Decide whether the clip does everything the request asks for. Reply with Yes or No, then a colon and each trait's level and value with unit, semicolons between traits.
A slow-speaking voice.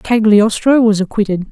Yes: slow, 120 wpm